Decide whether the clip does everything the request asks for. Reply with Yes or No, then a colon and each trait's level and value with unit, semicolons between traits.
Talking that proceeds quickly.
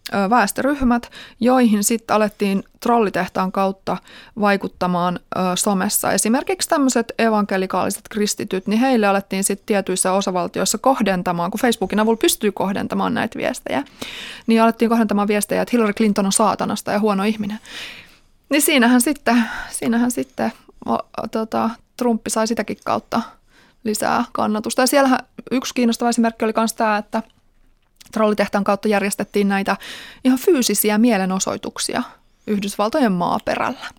No: average, 125 wpm